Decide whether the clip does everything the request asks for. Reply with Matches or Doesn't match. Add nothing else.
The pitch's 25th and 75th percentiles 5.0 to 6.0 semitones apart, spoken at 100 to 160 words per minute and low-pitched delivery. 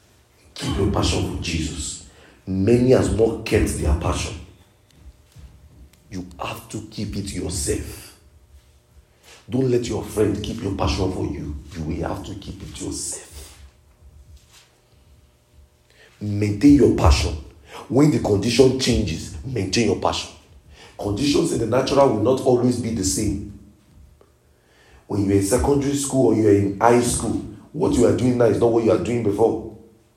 Matches